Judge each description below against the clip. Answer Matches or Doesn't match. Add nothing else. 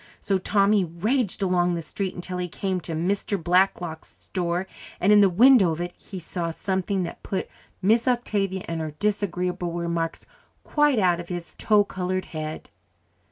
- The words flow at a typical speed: Matches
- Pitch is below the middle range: Doesn't match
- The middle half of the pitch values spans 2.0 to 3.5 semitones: Matches